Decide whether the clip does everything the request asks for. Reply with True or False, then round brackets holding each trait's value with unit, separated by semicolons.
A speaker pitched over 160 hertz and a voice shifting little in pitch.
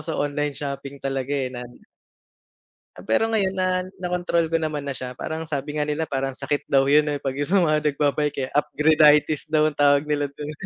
False (150 Hz; 2.1 semitones)